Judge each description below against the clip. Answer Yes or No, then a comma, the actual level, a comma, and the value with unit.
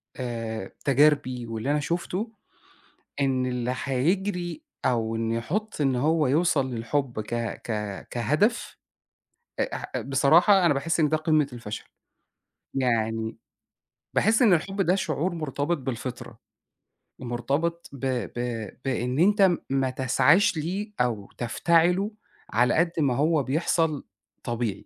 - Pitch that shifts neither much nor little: No, wide, 5.7 semitones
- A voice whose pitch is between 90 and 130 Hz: No, medium, 140 Hz